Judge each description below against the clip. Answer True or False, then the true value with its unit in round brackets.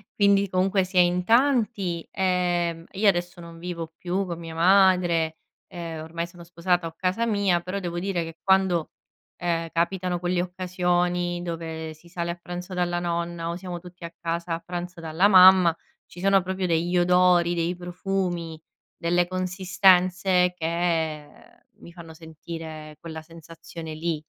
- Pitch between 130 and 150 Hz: False (175 Hz)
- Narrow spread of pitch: True (1.5 semitones)